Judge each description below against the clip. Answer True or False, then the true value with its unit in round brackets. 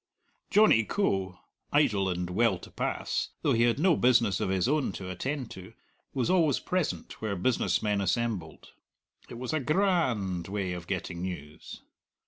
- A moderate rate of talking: True (165 wpm)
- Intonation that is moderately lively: False (6.3 semitones)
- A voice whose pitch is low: True (110 Hz)